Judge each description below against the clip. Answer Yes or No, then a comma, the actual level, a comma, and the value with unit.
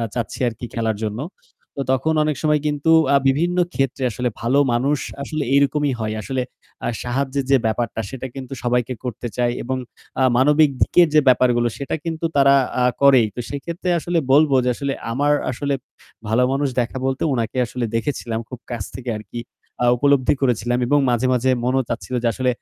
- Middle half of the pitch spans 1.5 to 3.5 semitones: Yes, average, 2.9 semitones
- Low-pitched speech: Yes, low, 130 Hz